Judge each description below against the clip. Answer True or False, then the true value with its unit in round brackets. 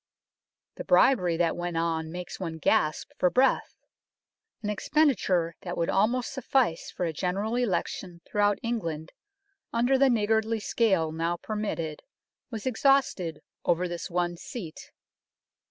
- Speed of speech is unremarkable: False (130 wpm)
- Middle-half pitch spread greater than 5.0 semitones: True (5.5 semitones)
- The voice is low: False (185 Hz)